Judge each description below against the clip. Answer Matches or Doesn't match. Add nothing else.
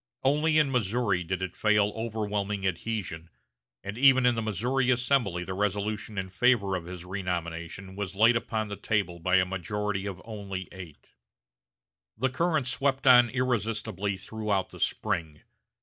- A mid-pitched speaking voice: Doesn't match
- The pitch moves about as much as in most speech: Matches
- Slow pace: Doesn't match